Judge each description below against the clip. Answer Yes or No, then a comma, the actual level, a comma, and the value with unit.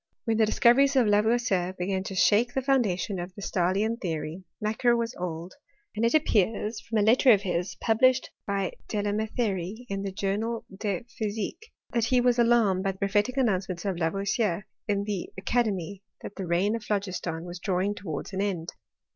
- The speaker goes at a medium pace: Yes, average, 180 wpm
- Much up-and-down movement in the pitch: No, average, 3.5 semitones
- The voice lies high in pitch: Yes, high, 205 Hz